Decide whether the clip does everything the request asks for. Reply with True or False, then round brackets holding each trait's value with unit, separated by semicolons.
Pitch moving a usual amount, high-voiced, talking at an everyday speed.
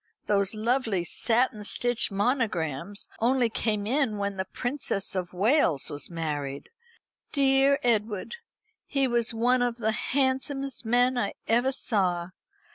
False (4.4 semitones; 225 Hz; 125 wpm)